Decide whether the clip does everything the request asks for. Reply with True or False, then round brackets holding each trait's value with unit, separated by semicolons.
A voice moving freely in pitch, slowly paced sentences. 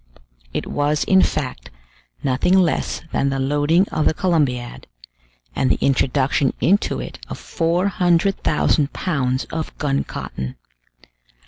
False (4.5 semitones; 120 wpm)